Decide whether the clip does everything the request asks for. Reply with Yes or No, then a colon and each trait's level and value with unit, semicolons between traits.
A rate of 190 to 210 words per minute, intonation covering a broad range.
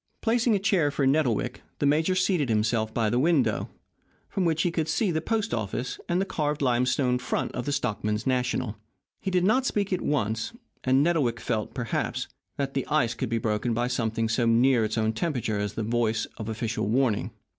Yes: average, 200 wpm; wide, 6.0 semitones